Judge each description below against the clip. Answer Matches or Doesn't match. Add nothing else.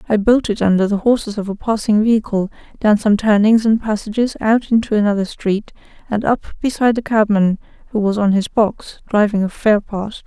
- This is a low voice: Doesn't match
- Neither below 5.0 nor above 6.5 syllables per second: Matches